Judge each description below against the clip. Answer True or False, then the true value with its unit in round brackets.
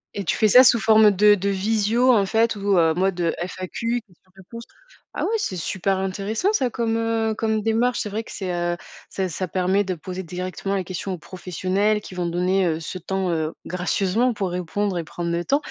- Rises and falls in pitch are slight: False (3.3 semitones)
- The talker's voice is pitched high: True (195 Hz)